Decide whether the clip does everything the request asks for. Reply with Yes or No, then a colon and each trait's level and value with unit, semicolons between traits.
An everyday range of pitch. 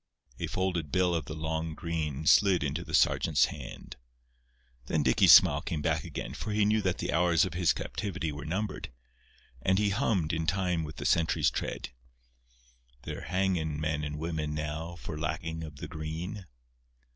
Yes: average, 3.0 semitones